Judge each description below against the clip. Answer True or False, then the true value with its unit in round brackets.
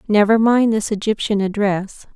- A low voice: False (210 Hz)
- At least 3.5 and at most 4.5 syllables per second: False (4.7 syllables/s)